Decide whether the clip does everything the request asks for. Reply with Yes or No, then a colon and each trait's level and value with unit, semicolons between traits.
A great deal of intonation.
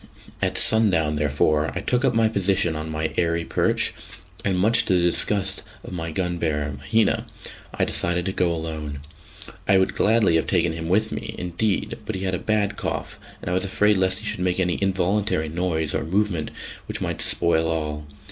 No: average, 3.8 semitones